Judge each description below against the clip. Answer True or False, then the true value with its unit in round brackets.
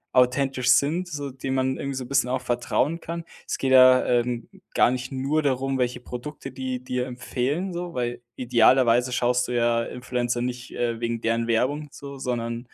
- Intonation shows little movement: True (1.9 semitones)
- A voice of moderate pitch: False (125 Hz)